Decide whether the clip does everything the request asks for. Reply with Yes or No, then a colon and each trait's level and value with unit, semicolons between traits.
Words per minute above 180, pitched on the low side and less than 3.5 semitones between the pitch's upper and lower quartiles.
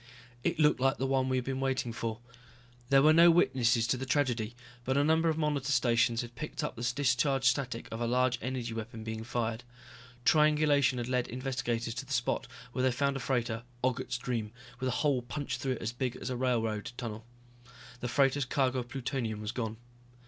Yes: fast, 205 wpm; low, 125 Hz; narrow, 2.5 semitones